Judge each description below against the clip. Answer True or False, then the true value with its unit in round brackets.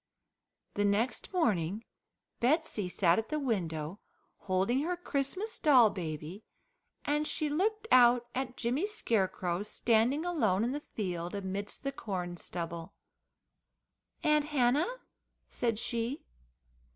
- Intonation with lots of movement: True (7.5 semitones)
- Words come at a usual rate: False (115 wpm)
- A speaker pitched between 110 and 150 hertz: False (235 Hz)